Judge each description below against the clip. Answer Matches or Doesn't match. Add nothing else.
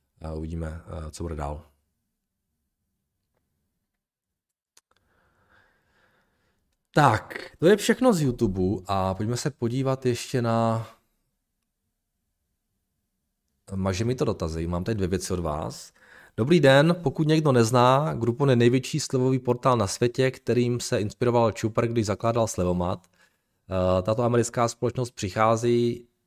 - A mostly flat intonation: Doesn't match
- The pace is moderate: Doesn't match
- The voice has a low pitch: Matches